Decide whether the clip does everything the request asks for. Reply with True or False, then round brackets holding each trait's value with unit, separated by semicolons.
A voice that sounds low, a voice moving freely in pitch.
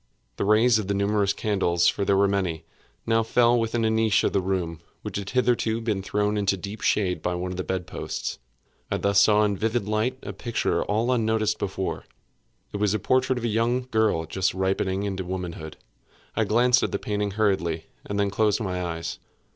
False (105 Hz; 2.8 semitones)